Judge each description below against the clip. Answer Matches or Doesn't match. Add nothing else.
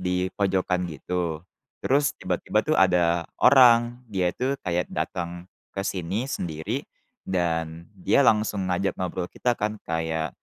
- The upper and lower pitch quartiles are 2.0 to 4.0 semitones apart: Matches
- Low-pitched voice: Matches